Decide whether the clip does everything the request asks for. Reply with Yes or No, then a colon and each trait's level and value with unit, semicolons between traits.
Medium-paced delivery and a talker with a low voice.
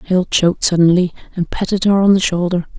No: average, 195 wpm; medium, 180 Hz